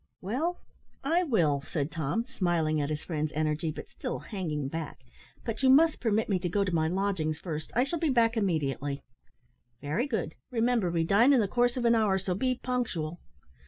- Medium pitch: No, high, 195 Hz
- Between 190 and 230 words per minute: Yes, average, 195 wpm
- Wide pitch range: Yes, wide, 7.5 semitones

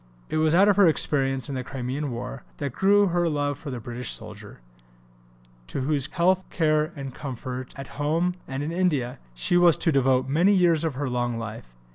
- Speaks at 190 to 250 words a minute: Yes, average, 195 wpm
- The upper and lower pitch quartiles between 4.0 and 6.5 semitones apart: Yes, average, 4.6 semitones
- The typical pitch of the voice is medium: Yes, medium, 145 Hz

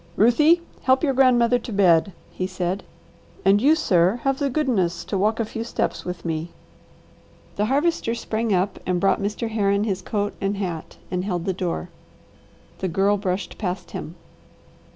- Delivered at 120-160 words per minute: No, average, 170 wpm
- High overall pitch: Yes, high, 200 Hz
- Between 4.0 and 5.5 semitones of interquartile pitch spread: Yes, average, 4.3 semitones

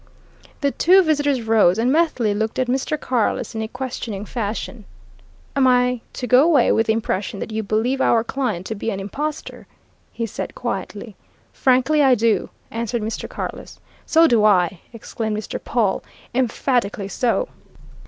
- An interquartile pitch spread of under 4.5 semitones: Yes, average, 3.4 semitones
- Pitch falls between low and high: No, high, 235 Hz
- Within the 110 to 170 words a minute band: Yes, average, 160 wpm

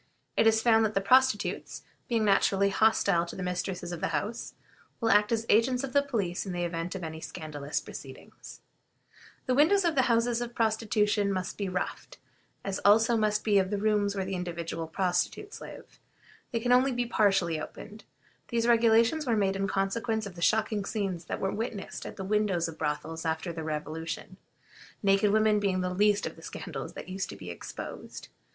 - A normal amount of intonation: Yes, average, 3.9 semitones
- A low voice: No, high, 200 Hz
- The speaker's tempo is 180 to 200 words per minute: Yes, average, 185 wpm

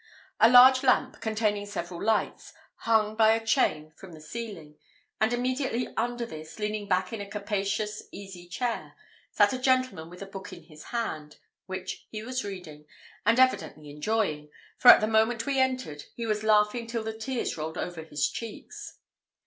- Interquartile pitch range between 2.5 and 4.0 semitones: No, average, 4.7 semitones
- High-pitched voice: Yes, high, 215 Hz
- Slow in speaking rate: No, average, 175 wpm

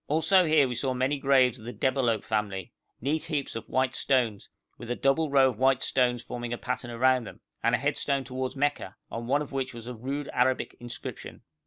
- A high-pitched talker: No, low, 130 Hz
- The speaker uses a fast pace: Yes, fast, 210 wpm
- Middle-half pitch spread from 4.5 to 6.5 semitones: No, narrow, 2.5 semitones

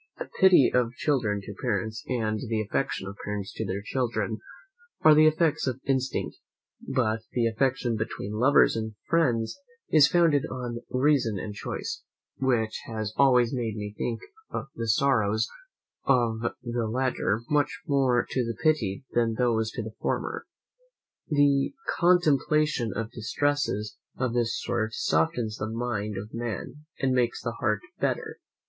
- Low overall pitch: Yes, low, 120 Hz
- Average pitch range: Yes, average, 3.7 semitones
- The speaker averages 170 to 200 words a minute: No, average, 145 wpm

